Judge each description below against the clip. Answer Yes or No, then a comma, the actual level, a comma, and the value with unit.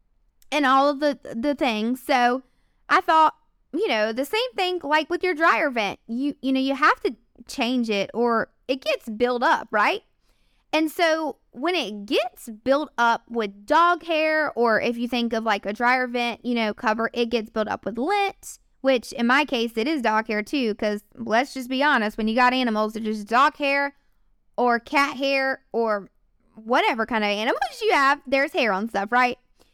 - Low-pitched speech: No, very high, 250 Hz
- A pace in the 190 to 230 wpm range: Yes, average, 200 wpm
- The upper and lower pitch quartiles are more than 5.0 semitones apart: No, average, 4.5 semitones